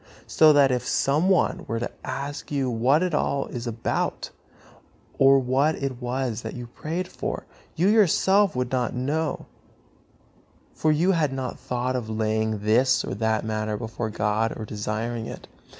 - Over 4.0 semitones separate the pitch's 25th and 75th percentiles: Yes, average, 4.6 semitones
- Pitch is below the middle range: Yes, low, 125 Hz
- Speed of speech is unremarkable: Yes, average, 165 wpm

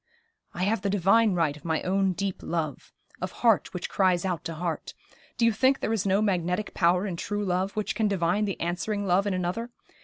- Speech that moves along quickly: Yes, fast, 215 wpm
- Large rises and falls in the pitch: No, average, 2.9 semitones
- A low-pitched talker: No, high, 190 Hz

